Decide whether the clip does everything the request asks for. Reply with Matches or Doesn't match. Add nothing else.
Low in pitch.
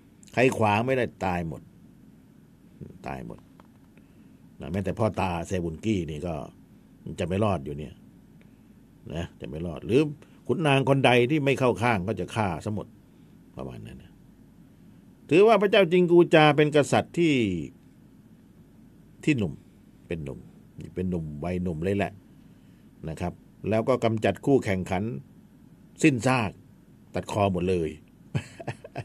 Matches